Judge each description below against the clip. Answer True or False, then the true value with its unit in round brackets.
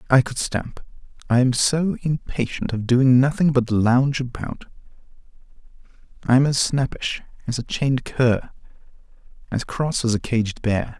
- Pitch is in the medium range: False (125 Hz)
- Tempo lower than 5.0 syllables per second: True (4.6 syllables/s)